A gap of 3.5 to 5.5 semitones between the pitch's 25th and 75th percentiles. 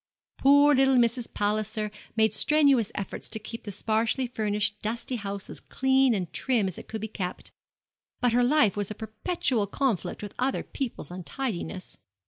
Yes: average, 4.0 semitones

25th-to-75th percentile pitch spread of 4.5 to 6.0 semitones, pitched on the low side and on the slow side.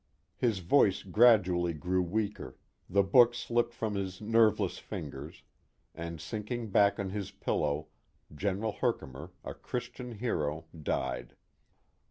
Yes: average, 4.8 semitones; low, 100 Hz; slow, 120 wpm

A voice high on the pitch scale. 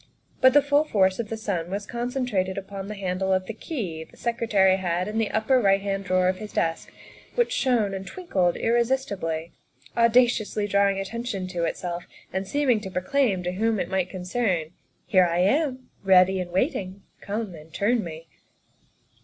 Yes: high, 195 Hz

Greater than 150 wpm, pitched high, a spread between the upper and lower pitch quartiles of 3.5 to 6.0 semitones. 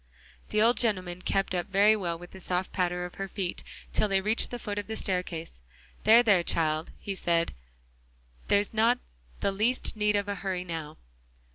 No: average, 180 wpm; high, 195 Hz; average, 3.0 semitones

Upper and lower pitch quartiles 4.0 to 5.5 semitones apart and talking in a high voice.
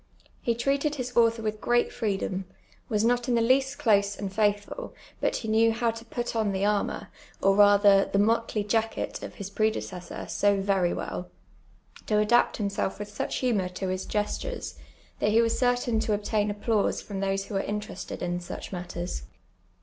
No: average, 2.7 semitones; high, 210 Hz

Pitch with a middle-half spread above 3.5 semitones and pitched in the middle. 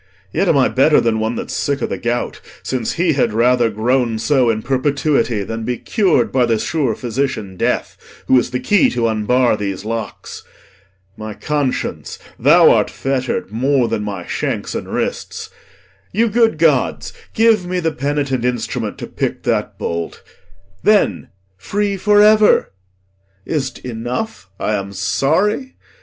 No: wide, 5.4 semitones; low, 125 Hz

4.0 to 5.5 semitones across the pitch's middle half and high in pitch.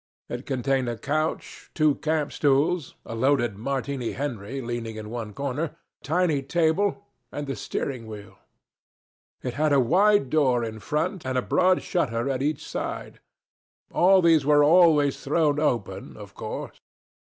No: average, 4.3 semitones; medium, 140 Hz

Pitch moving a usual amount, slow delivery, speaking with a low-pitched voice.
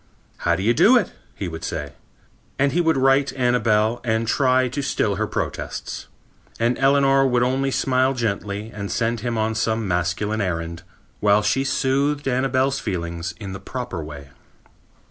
No: average, 4.9 semitones; average, 165 wpm; low, 115 Hz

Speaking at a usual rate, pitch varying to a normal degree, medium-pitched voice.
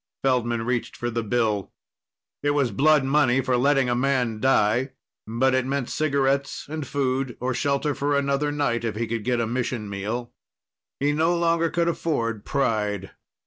No: average, 170 wpm; average, 3.3 semitones; low, 130 Hz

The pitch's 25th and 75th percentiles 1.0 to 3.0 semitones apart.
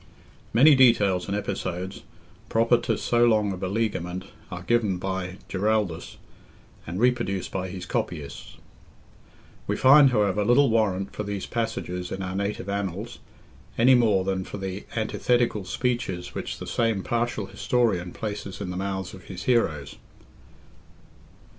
No: average, 3.9 semitones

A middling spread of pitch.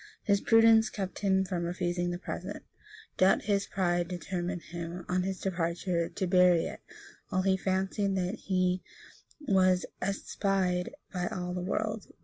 No: narrow, 1.6 semitones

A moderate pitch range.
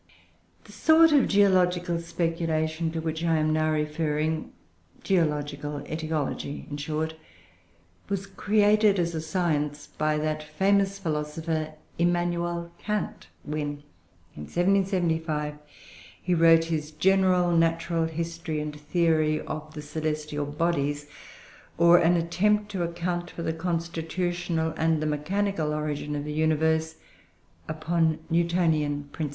No: narrow, 2.2 semitones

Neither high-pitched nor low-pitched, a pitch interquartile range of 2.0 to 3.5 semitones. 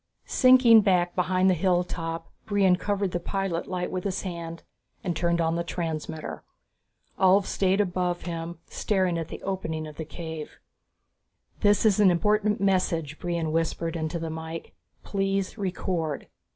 Yes: medium, 180 Hz; average, 2.8 semitones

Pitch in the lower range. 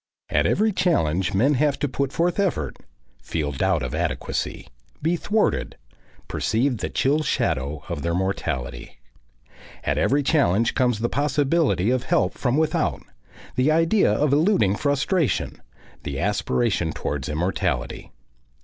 Yes: low, 130 Hz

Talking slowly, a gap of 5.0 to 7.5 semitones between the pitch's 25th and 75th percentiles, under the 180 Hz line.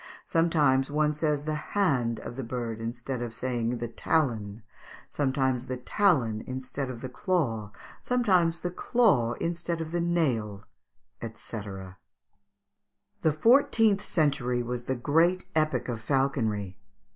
Yes: slow, 130 wpm; wide, 5.6 semitones; low, 135 Hz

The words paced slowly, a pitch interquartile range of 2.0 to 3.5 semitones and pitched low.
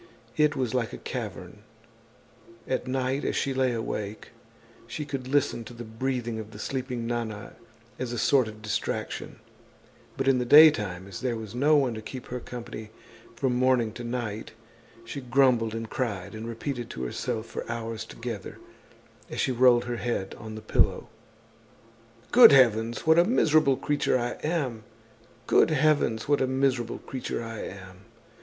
No: average, 165 wpm; average, 2.9 semitones; low, 120 Hz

